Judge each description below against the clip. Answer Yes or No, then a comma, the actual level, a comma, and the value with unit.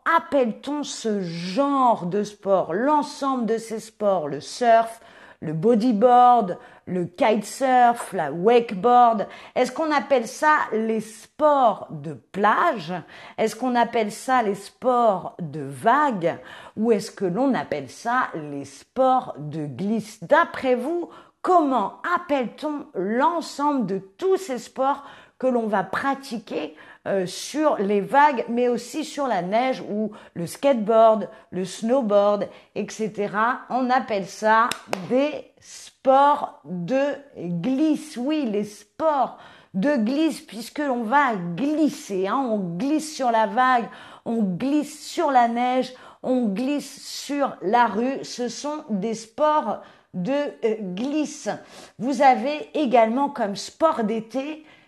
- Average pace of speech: No, slow, 125 wpm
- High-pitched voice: Yes, high, 240 Hz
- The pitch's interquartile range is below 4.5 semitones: No, average, 5.1 semitones